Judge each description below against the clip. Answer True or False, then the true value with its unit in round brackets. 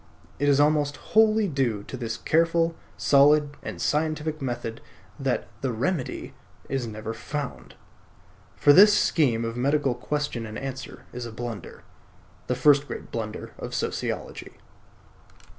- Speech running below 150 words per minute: True (135 wpm)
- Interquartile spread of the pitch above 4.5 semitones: False (4.0 semitones)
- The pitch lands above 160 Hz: False (140 Hz)